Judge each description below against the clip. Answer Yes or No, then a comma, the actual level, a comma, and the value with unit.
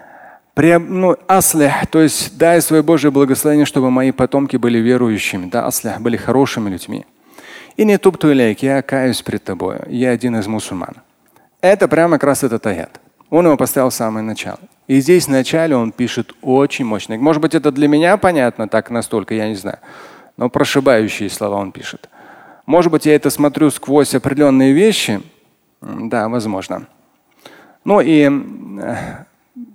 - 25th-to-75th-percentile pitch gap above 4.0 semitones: Yes, average, 5.2 semitones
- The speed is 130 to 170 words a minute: Yes, fast, 160 wpm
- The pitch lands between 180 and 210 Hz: No, low, 135 Hz